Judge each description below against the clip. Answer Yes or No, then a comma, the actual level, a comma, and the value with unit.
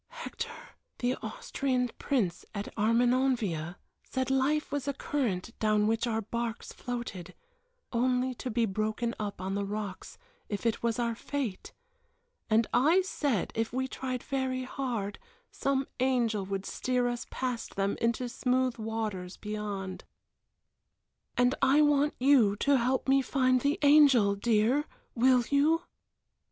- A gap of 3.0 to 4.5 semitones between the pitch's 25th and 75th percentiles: Yes, average, 3.7 semitones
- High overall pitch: Yes, high, 245 Hz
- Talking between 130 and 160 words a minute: Yes, average, 140 wpm